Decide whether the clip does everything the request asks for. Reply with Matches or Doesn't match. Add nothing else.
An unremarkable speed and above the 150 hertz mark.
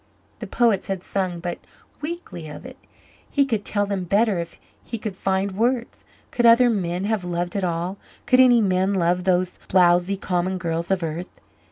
Matches